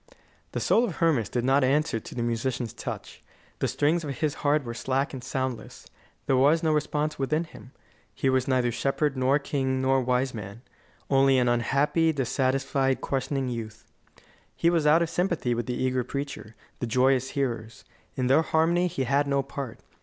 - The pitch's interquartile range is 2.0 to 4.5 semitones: Yes, average, 2.8 semitones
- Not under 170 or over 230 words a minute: Yes, average, 180 wpm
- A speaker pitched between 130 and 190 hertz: Yes, low, 135 Hz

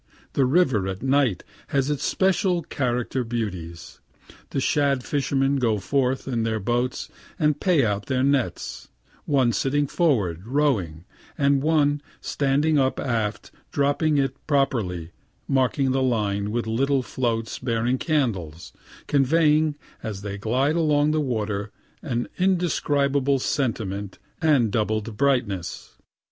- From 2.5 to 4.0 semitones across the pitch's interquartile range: No, average, 4.6 semitones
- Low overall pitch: Yes, low, 130 Hz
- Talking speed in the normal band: No, slow, 125 wpm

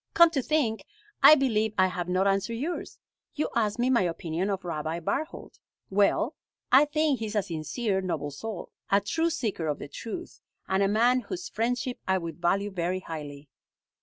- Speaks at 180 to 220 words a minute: Yes, average, 185 wpm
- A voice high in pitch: Yes, high, 205 Hz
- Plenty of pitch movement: Yes, wide, 5.9 semitones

